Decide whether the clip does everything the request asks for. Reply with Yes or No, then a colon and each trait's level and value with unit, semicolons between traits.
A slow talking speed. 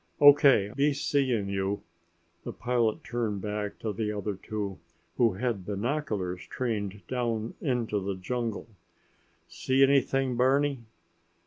Yes: slow, 120 wpm